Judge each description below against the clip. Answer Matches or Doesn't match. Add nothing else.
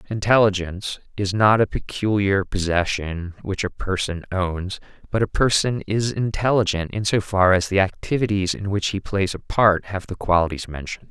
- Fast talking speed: Doesn't match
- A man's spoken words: Matches